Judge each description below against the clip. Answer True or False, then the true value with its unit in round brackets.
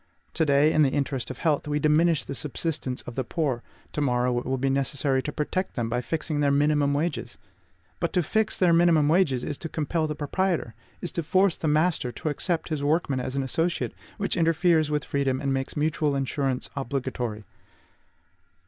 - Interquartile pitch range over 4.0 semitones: False (3.3 semitones)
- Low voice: False (145 Hz)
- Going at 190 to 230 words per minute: True (195 wpm)